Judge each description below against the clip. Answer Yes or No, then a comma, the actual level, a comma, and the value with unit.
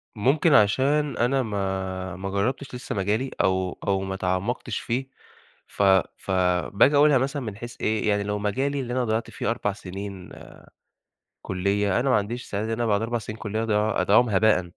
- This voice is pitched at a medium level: No, low, 105 Hz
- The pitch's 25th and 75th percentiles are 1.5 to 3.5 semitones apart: No, average, 3.9 semitones